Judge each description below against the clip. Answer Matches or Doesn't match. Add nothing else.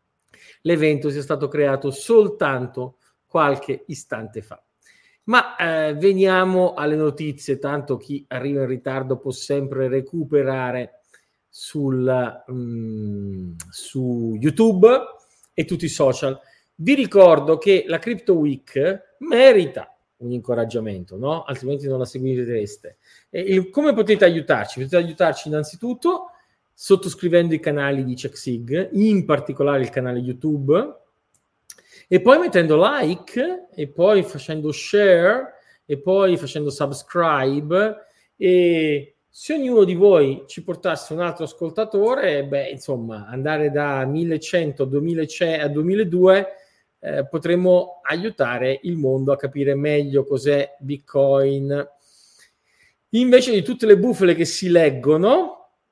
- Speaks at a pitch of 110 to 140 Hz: Doesn't match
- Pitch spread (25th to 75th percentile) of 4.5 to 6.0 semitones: Matches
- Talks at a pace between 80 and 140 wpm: Matches